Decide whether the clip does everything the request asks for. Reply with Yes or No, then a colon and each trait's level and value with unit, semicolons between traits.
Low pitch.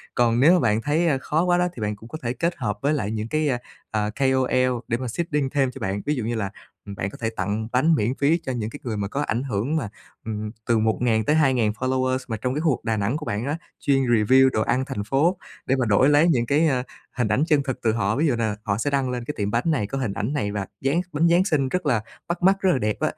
Yes: low, 130 Hz